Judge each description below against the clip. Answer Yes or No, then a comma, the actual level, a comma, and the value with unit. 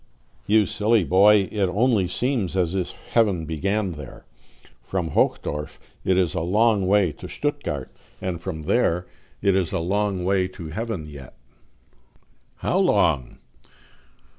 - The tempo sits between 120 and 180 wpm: Yes, average, 140 wpm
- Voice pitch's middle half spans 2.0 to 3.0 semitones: No, average, 4.1 semitones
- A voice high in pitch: No, very low, 95 Hz